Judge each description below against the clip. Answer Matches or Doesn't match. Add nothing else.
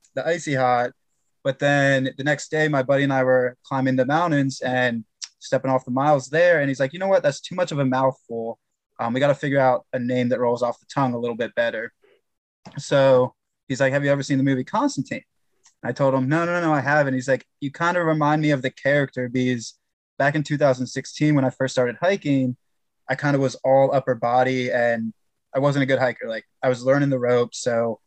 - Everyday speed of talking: Doesn't match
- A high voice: Doesn't match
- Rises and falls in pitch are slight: Matches